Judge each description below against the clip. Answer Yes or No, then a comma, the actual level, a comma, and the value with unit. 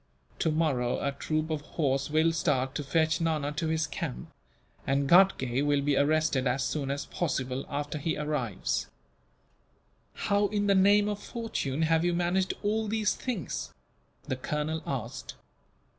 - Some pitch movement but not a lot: Yes, average, 4.1 semitones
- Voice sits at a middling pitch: Yes, medium, 155 Hz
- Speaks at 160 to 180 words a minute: No, average, 150 wpm